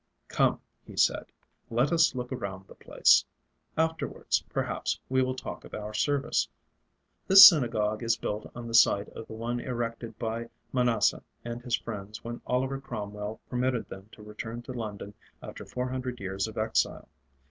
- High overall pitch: No, low, 115 Hz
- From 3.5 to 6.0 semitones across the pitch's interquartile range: No, average, 2.8 semitones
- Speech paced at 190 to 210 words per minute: No, average, 165 wpm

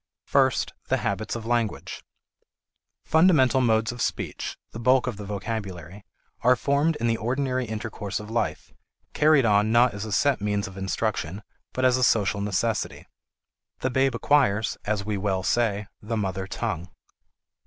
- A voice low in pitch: Yes, low, 110 Hz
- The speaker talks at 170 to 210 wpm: No, average, 155 wpm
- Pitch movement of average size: Yes, average, 3.9 semitones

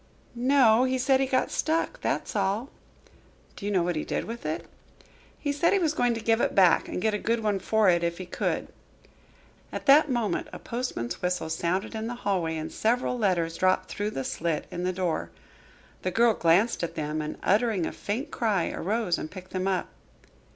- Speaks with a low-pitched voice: No, high, 205 Hz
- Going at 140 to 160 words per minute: No, fast, 205 wpm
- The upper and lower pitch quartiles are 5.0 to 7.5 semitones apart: Yes, average, 5.3 semitones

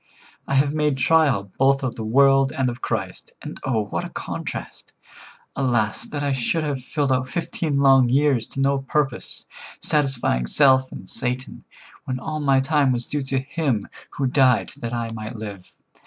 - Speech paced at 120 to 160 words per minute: No, average, 175 wpm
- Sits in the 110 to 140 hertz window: Yes, low, 135 Hz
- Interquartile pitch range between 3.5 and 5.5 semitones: No, average, 2.7 semitones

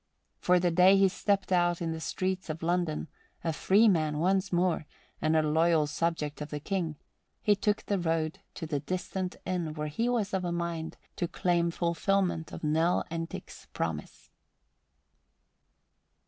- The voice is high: No, medium, 170 Hz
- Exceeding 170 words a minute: No, average, 160 wpm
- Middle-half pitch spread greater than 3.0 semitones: No, narrow, 2.6 semitones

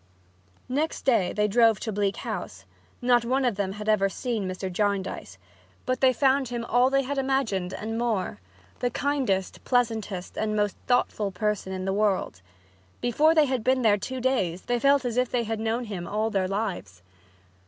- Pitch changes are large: No, average, 4.3 semitones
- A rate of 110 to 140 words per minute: No, average, 185 wpm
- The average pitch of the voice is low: No, high, 225 Hz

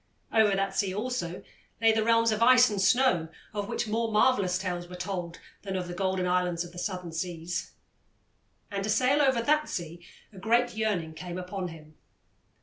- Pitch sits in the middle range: No, high, 195 Hz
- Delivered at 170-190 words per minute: Yes, average, 185 wpm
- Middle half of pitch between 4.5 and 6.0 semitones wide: No, average, 4.1 semitones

